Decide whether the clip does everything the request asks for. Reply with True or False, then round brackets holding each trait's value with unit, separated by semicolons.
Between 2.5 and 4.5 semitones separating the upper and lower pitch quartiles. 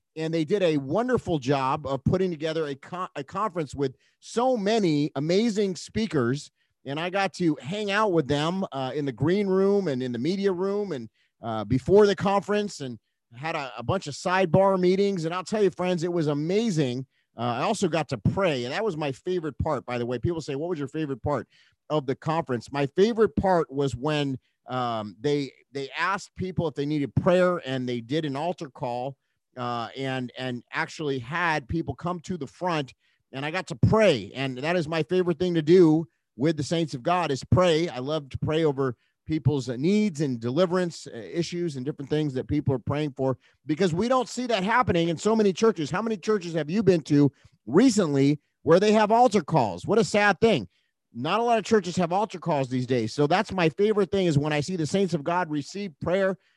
False (5.3 semitones)